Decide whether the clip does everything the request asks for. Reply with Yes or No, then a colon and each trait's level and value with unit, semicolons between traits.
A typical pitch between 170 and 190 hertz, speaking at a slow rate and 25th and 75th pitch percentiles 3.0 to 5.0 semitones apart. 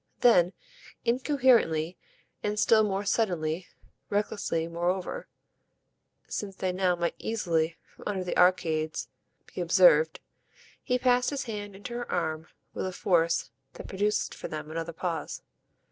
Yes: medium, 185 Hz; slow, 130 wpm; average, 4.1 semitones